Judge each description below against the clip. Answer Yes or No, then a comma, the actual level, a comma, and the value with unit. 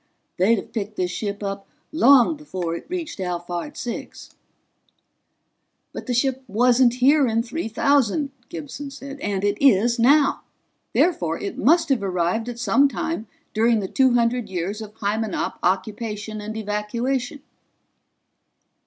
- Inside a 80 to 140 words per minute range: Yes, slow, 135 wpm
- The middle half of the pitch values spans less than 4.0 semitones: No, average, 4.8 semitones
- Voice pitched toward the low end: No, high, 225 Hz